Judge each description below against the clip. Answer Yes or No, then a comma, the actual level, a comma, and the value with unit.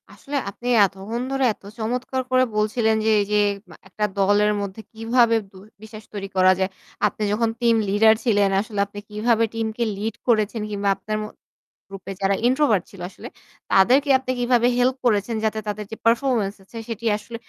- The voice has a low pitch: No, high, 220 Hz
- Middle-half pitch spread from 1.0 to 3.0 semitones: Yes, narrow, 2.6 semitones